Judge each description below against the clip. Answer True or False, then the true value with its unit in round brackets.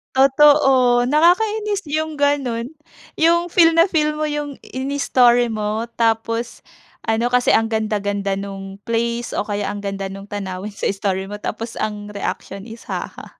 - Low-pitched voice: False (235 Hz)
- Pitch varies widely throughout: True (6.0 semitones)